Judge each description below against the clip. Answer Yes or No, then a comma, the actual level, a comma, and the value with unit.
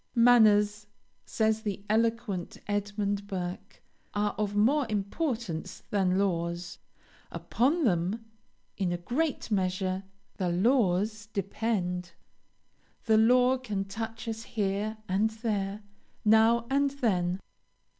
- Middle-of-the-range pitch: No, high, 210 Hz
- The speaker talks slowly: Yes, slow, 105 wpm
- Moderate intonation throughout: Yes, average, 3.0 semitones